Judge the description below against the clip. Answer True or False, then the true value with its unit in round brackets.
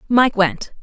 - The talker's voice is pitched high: True (200 Hz)